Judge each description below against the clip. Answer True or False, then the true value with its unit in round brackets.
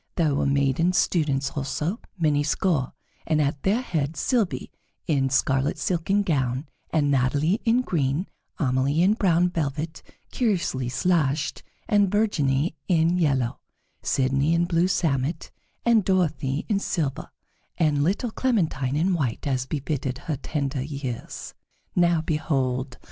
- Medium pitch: True (155 Hz)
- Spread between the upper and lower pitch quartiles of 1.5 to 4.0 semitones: False (4.5 semitones)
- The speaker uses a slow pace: True (130 wpm)